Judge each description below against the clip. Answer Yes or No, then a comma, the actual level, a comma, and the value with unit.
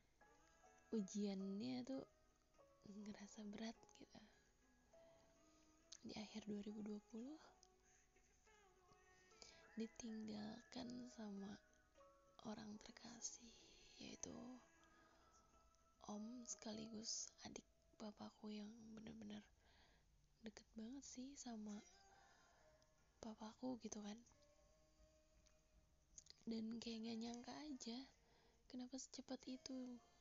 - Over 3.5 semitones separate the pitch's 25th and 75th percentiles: No, average, 3.2 semitones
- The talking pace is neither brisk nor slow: No, slow, 70 wpm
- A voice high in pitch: Yes, high, 225 Hz